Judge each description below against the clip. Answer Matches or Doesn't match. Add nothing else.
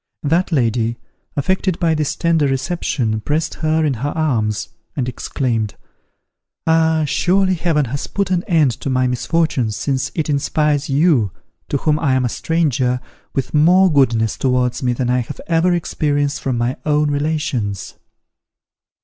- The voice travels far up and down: Doesn't match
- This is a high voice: Doesn't match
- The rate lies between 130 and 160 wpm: Matches